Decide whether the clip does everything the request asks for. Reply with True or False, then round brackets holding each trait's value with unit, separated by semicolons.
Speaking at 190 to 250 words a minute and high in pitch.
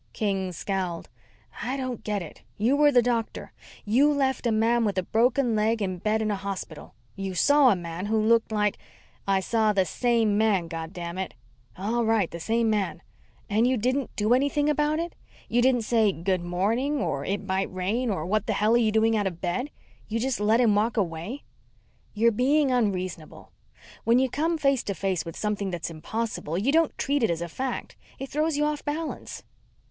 True (200 wpm; 220 Hz)